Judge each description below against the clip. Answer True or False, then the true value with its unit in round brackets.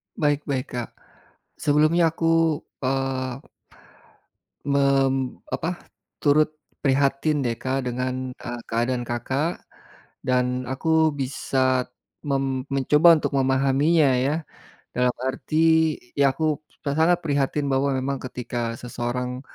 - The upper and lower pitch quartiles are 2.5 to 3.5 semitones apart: True (2.8 semitones)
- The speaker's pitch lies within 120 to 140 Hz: True (135 Hz)